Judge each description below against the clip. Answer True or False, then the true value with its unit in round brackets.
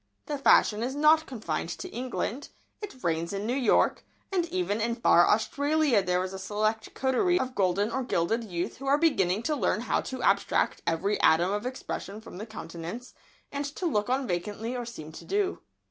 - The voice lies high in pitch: True (225 Hz)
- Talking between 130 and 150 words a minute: False (195 wpm)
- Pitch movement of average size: False (5.7 semitones)